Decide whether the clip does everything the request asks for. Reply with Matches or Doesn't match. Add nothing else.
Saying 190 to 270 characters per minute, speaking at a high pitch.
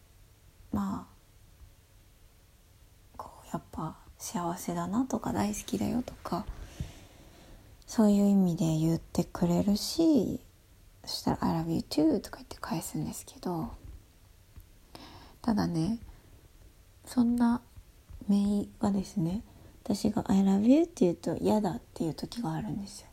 Doesn't match